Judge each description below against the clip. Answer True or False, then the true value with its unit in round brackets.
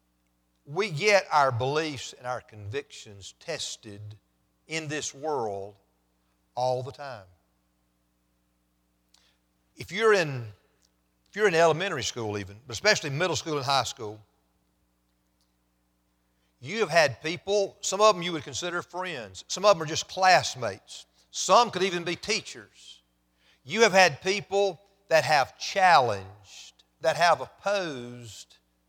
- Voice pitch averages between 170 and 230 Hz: False (115 Hz)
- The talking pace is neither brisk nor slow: False (130 wpm)